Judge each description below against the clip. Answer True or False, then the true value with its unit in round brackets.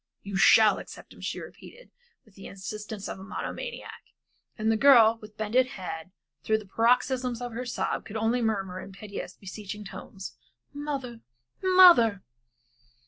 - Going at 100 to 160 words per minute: True (150 wpm)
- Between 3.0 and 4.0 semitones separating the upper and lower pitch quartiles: True (3.7 semitones)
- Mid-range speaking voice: False (220 Hz)